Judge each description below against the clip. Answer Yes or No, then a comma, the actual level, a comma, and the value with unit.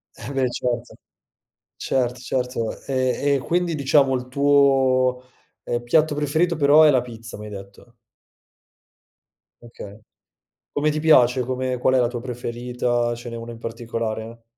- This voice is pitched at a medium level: No, low, 125 Hz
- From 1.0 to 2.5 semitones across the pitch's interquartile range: No, average, 2.9 semitones